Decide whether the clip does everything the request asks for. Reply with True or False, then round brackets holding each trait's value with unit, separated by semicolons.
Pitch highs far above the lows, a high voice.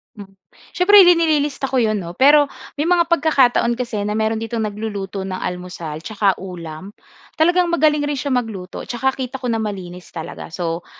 True (7.1 semitones; 225 Hz)